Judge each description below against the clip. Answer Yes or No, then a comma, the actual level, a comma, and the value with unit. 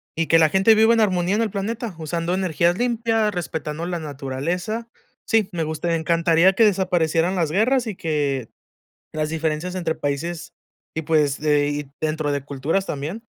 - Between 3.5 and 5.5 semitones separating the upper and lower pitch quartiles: Yes, average, 4.0 semitones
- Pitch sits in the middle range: Yes, medium, 170 Hz